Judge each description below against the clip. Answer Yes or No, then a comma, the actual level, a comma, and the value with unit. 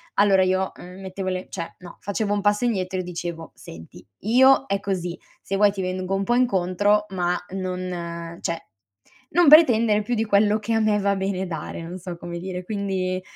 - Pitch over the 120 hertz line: Yes, high, 190 Hz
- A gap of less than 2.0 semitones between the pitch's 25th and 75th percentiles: No, narrow, 2.5 semitones